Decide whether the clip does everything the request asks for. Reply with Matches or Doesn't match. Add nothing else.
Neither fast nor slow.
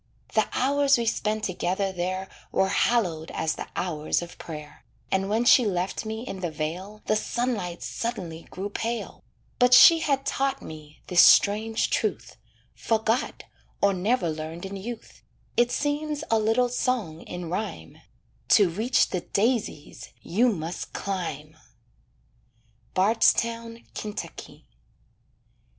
Doesn't match